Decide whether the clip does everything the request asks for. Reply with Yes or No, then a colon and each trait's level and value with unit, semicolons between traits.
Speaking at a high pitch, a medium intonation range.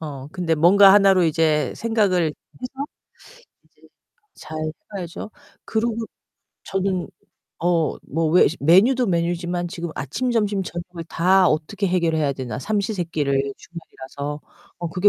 No: medium, 175 Hz; average, 3.6 semitones